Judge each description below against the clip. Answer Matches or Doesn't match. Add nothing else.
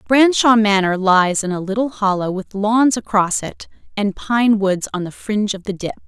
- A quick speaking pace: Doesn't match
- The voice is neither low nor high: Doesn't match